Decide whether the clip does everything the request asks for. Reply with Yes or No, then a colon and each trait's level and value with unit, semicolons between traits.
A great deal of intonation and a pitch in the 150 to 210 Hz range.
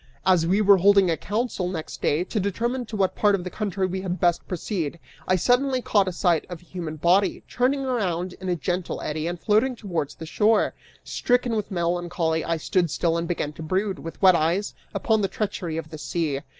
No: average, 3.6 semitones; medium, 185 Hz